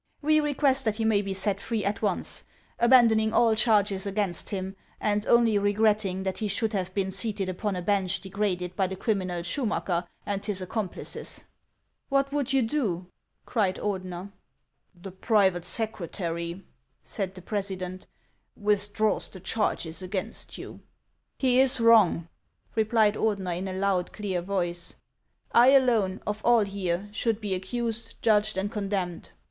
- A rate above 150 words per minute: Yes, average, 165 wpm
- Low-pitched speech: No, high, 200 Hz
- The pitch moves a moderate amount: Yes, average, 3.0 semitones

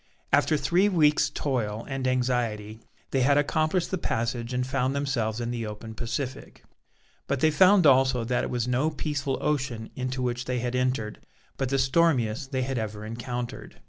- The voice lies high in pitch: No, low, 130 Hz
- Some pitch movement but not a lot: Yes, average, 3.0 semitones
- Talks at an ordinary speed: Yes, average, 175 wpm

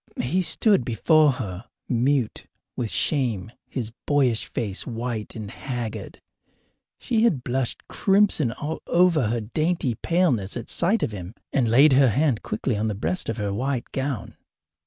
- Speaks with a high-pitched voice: No, low, 125 Hz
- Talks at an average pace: Yes, average, 155 wpm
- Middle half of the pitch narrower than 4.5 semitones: No, average, 5.3 semitones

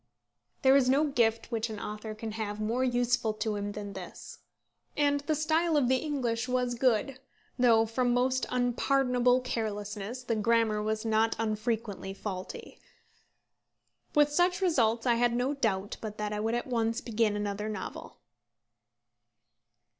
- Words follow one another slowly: No, average, 150 wpm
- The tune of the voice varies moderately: Yes, average, 3.0 semitones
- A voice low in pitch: No, high, 230 Hz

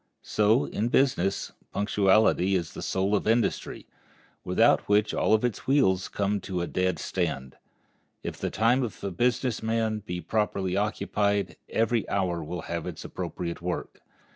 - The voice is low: Yes, low, 100 Hz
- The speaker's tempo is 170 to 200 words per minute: No, average, 150 wpm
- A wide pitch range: No, average, 3.3 semitones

